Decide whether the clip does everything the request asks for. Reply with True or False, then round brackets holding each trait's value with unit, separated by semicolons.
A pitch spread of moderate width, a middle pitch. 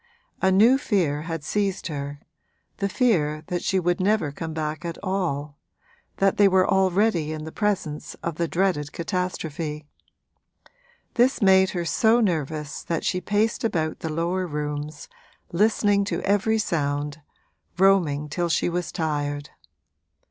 True (4.4 semitones; 170 Hz)